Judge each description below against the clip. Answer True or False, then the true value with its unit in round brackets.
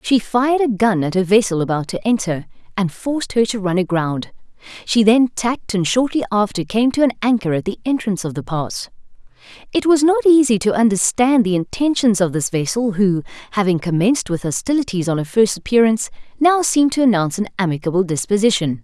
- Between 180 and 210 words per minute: True (190 wpm)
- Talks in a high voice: True (210 Hz)